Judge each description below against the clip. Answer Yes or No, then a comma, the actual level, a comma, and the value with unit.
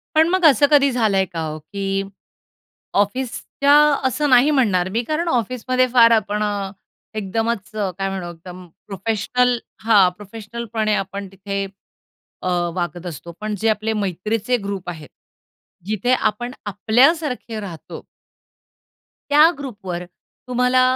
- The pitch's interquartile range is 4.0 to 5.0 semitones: Yes, average, 4.4 semitones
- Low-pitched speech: No, high, 215 Hz